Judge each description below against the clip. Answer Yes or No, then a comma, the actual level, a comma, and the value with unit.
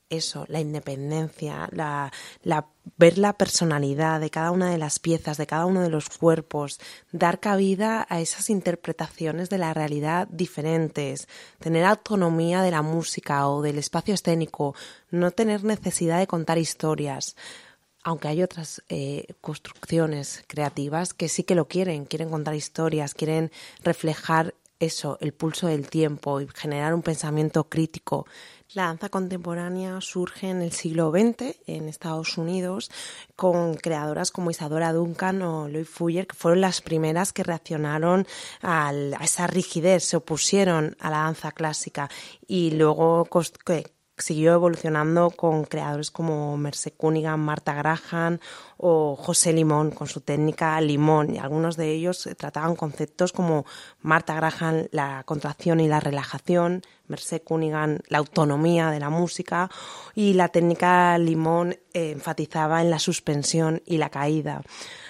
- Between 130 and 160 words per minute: Yes, average, 145 wpm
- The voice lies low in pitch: No, medium, 165 Hz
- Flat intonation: Yes, narrow, 2.3 semitones